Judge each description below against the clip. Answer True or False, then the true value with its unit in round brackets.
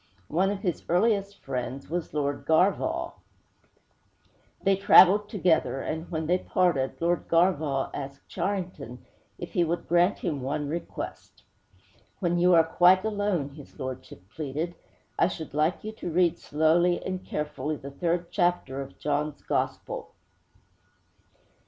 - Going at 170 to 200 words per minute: False (135 wpm)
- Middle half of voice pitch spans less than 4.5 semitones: True (4.0 semitones)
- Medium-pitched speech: True (170 Hz)